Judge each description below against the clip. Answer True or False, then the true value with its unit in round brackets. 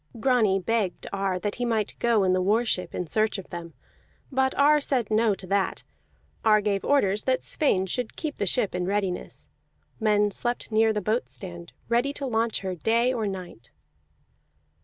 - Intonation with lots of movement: False (3.8 semitones)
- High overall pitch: True (215 Hz)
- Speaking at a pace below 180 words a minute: False (185 wpm)